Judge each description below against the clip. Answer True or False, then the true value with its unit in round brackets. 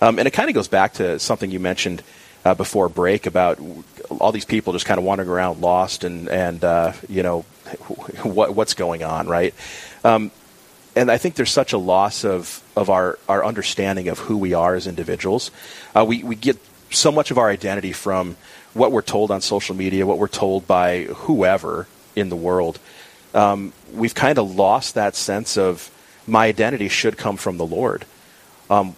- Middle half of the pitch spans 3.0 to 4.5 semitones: False (2.6 semitones)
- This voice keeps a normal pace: True (195 wpm)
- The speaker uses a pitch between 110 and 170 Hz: False (95 Hz)